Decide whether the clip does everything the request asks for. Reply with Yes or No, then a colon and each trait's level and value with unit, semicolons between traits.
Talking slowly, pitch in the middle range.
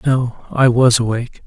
No: slow, 125 wpm; low, 125 Hz